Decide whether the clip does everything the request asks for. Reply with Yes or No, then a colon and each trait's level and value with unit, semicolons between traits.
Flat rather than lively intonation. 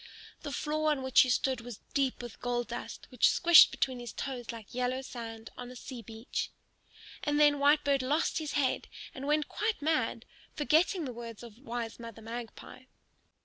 No: average, 3.6 semitones